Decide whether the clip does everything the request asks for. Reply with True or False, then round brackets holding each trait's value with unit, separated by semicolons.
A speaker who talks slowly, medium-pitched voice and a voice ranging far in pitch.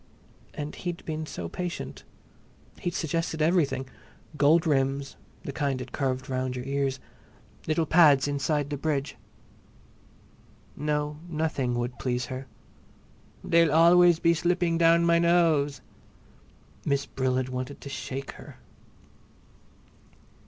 False (115 wpm; 145 Hz; 3.7 semitones)